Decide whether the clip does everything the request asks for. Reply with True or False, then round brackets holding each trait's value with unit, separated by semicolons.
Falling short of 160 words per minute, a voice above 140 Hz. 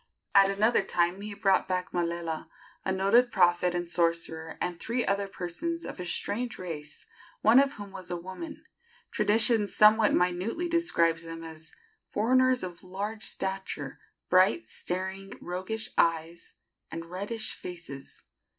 True (140 wpm; 185 Hz)